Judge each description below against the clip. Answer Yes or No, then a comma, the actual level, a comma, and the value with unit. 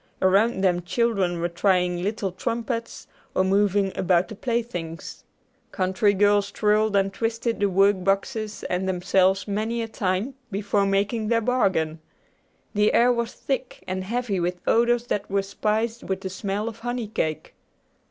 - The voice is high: Yes, high, 200 Hz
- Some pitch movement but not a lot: Yes, average, 3.4 semitones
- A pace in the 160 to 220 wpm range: No, average, 150 wpm